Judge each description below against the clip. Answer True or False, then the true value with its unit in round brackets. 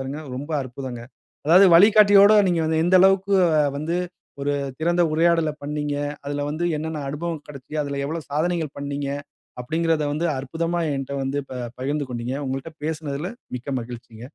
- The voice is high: False (150 Hz)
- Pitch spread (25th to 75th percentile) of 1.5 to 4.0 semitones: True (3.3 semitones)